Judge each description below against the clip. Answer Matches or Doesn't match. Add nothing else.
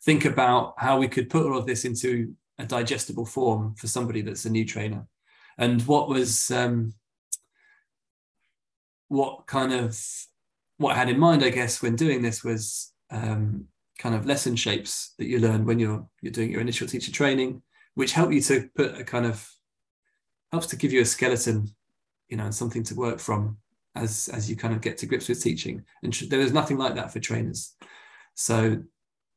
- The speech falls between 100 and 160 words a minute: Doesn't match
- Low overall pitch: Matches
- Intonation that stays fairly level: Doesn't match